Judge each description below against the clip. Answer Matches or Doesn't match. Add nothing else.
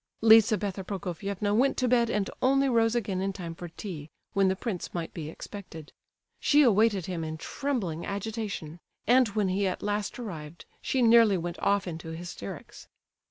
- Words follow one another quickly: Doesn't match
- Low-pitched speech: Doesn't match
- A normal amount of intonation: Matches